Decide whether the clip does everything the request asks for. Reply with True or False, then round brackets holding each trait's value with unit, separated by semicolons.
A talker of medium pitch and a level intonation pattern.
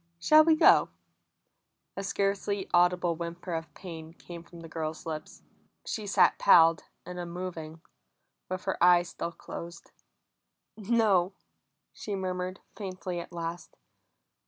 True (175 Hz; 2.3 semitones)